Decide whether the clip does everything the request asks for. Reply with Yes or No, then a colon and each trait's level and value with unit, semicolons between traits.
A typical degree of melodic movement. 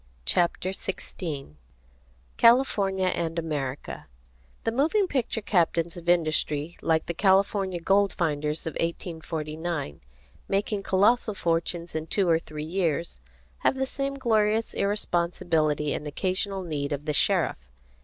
Yes: average, 4.0 semitones